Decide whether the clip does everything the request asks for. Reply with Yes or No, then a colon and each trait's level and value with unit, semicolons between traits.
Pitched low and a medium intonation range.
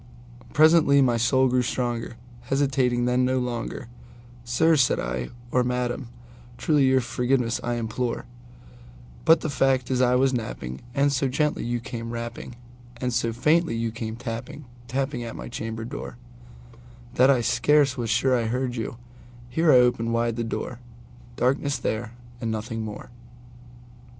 No: low, 120 Hz; narrow, 2.0 semitones